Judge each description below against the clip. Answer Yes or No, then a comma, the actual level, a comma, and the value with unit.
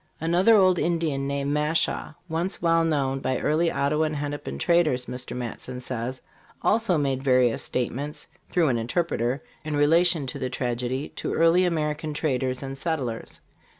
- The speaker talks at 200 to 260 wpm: No, average, 150 wpm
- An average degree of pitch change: Yes, average, 4.3 semitones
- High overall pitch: No, medium, 145 Hz